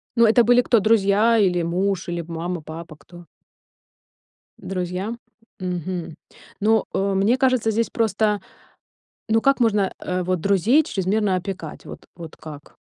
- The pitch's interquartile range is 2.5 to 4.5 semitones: Yes, average, 4.0 semitones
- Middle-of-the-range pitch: No, high, 195 Hz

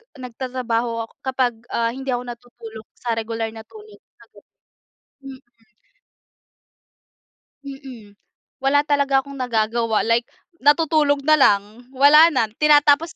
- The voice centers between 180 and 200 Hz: No, very high, 255 Hz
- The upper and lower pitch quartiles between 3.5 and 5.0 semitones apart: Yes, average, 3.8 semitones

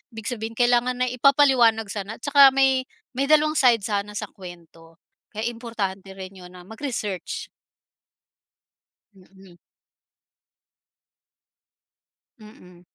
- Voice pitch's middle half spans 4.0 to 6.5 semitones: Yes, average, 4.7 semitones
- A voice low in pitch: No, high, 220 Hz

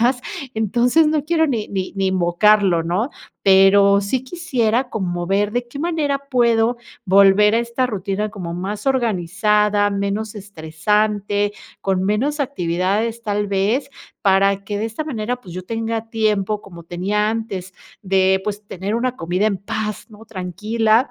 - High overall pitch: Yes, high, 210 Hz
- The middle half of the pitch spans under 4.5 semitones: Yes, average, 3.2 semitones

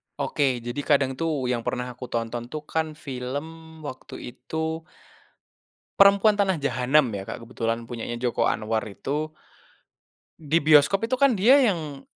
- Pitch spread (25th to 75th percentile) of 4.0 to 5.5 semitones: Yes, average, 4.7 semitones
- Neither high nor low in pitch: Yes, medium, 145 Hz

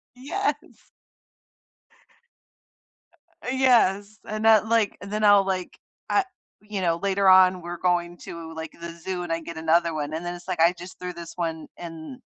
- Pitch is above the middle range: No, medium, 180 Hz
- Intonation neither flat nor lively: Yes, average, 3.4 semitones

